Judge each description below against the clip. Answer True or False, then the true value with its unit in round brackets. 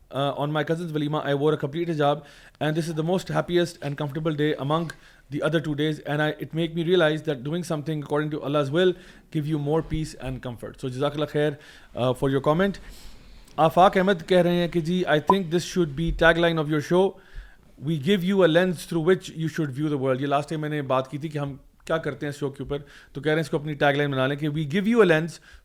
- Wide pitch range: False (2.6 semitones)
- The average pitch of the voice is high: False (155 Hz)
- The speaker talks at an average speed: False (230 wpm)